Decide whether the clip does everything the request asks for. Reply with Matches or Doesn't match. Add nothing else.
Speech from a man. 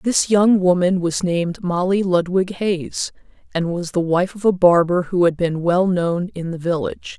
Doesn't match